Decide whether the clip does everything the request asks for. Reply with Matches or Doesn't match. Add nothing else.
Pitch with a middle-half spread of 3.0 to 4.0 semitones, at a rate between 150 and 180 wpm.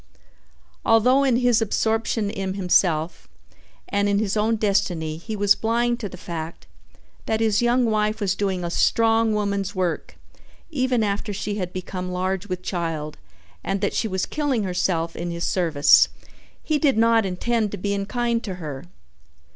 Matches